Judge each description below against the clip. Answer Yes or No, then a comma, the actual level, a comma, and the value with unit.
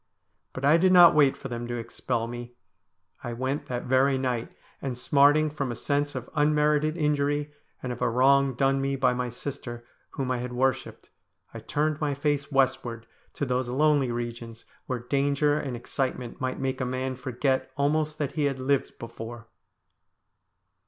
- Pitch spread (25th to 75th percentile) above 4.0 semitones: No, average, 2.7 semitones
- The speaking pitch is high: No, low, 135 Hz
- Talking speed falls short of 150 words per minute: No, average, 175 wpm